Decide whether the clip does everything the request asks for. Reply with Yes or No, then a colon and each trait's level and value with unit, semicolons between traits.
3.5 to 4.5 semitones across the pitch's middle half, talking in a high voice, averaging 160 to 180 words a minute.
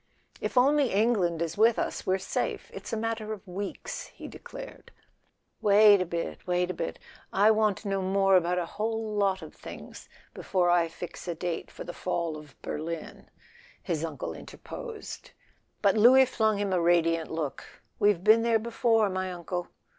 Yes: average, 4.0 semitones; high, 195 Hz; average, 170 wpm